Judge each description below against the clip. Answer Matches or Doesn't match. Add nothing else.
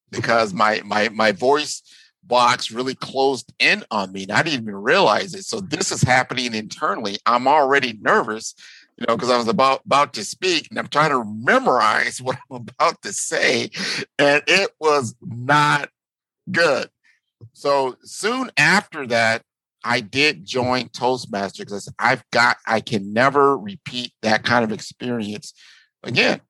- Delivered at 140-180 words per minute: Matches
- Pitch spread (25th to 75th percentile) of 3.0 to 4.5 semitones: Matches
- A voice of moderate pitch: Doesn't match